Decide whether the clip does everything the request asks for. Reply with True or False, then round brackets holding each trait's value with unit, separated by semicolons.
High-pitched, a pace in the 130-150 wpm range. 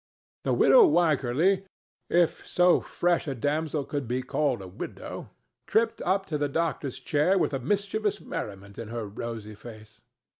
False (145 Hz; 145 wpm)